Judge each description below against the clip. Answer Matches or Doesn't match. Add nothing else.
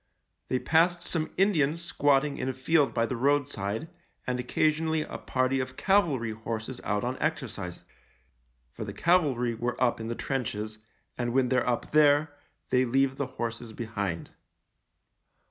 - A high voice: Doesn't match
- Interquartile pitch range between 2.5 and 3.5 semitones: Doesn't match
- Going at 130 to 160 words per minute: Matches